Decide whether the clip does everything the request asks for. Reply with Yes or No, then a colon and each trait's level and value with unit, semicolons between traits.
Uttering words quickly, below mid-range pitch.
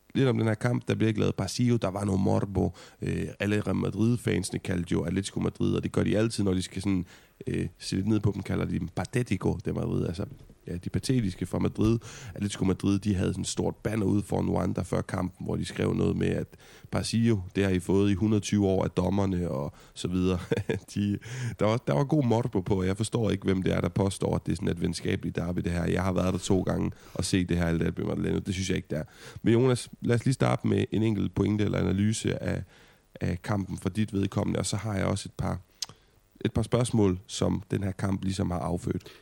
Yes: fast, 245 wpm; low, 100 Hz